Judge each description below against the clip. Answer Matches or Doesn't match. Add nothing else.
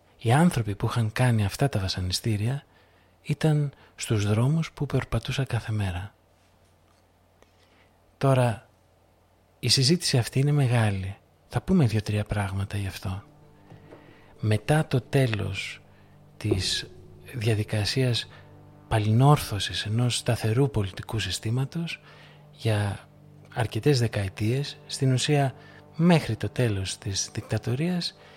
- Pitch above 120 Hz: Doesn't match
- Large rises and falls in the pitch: Matches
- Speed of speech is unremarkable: Doesn't match